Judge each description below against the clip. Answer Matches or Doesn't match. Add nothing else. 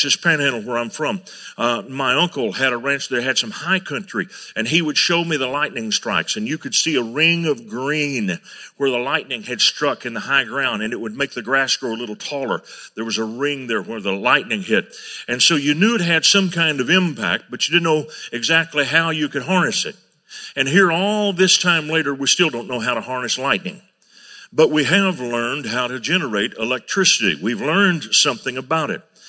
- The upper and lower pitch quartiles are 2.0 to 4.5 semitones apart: Doesn't match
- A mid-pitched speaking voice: Matches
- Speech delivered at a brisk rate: Matches